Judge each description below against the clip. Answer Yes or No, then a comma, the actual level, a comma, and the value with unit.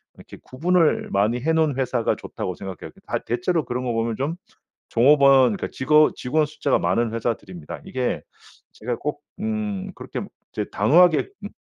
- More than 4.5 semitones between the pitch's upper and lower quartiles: Yes, average, 5.3 semitones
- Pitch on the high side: No, low, 130 Hz